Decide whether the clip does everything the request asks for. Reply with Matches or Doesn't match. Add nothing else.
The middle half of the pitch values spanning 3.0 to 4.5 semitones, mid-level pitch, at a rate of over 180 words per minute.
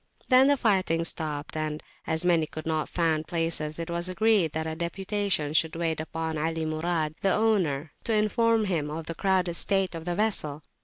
Matches